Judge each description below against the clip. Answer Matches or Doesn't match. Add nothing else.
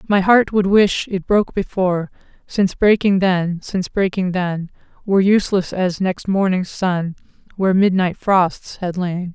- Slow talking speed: Doesn't match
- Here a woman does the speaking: Matches